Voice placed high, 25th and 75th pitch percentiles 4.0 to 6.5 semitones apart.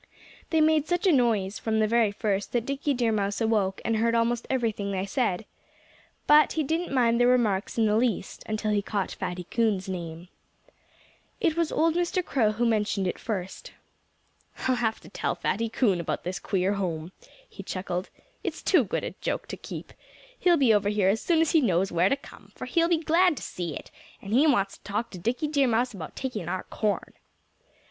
Yes: high, 225 Hz; average, 5.3 semitones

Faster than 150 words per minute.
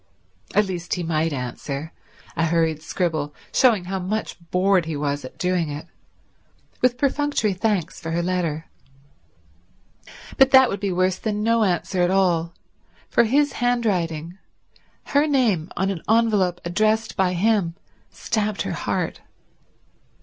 No: slow, 135 wpm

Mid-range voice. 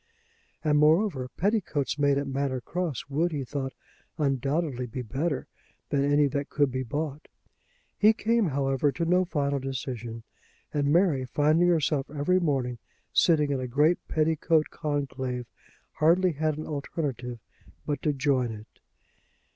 Yes: medium, 145 Hz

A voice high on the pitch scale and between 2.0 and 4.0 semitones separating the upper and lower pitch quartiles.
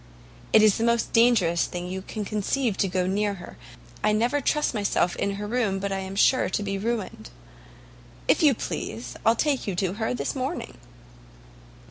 Yes: high, 205 Hz; average, 3.6 semitones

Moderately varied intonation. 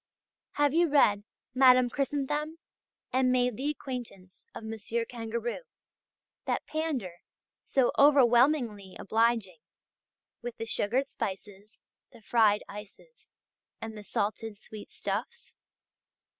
Yes: average, 4.4 semitones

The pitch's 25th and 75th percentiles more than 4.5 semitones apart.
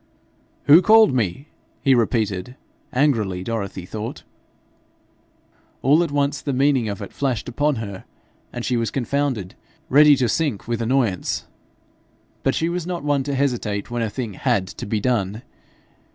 Yes: average, 5.0 semitones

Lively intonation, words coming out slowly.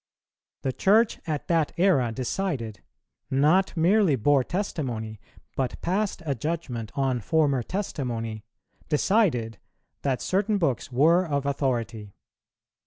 Yes: wide, 6.5 semitones; slow, 110 wpm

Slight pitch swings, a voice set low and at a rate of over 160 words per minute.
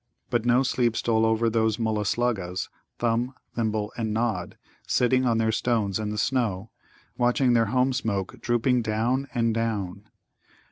No: narrow, 2.1 semitones; low, 115 Hz; average, 150 wpm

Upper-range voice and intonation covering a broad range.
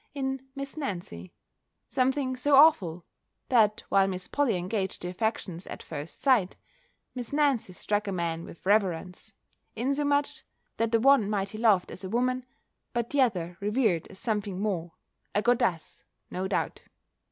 Yes: high, 210 Hz; wide, 5.8 semitones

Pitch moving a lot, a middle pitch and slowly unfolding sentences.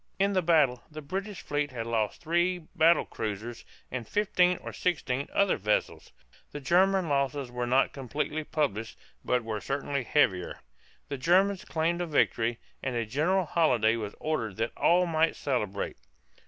No: wide, 6.4 semitones; medium, 145 Hz; average, 155 wpm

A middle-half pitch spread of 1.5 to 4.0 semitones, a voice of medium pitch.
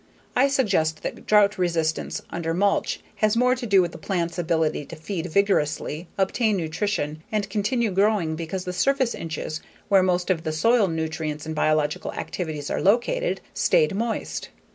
No: average, 4.8 semitones; medium, 180 Hz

